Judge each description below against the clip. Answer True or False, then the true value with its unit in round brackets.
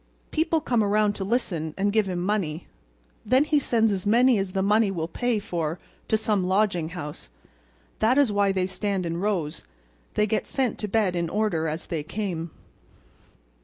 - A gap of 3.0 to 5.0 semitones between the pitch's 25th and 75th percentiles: True (3.7 semitones)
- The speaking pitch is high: True (200 Hz)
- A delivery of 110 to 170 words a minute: False (180 wpm)